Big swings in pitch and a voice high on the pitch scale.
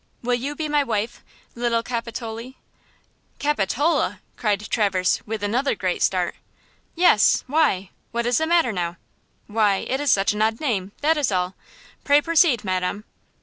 Yes: wide, 5.9 semitones; high, 230 Hz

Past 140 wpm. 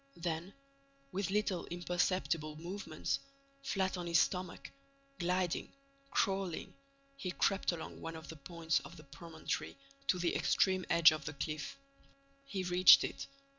No: slow, 135 wpm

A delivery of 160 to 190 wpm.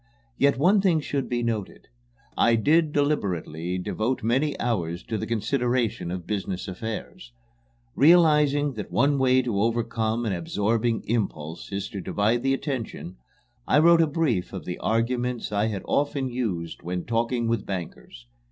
No: average, 150 wpm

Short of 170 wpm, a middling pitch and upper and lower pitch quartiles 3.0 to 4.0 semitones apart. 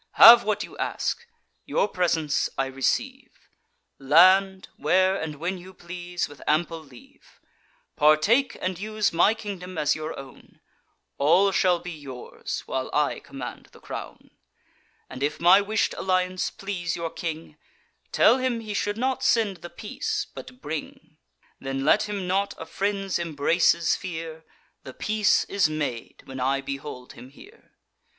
No: average, 145 wpm; medium, 175 Hz; average, 4.9 semitones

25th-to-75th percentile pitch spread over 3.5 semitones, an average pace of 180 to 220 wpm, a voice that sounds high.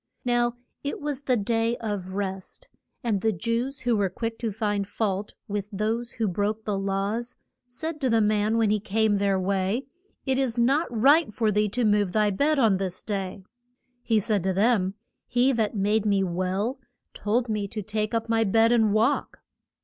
No: average, 2.9 semitones; average, 190 wpm; high, 215 Hz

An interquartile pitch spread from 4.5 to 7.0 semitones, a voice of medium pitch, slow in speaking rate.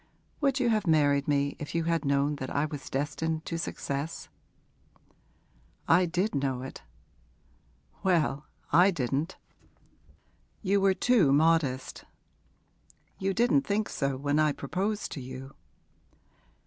Yes: average, 5.2 semitones; medium, 155 Hz; slow, 125 wpm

